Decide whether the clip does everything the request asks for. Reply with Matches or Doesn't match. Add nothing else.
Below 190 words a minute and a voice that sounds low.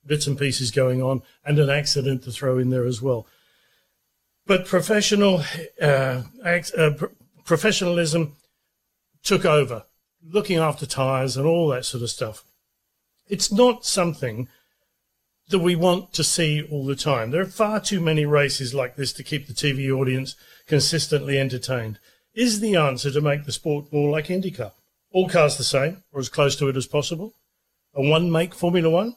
Doesn't match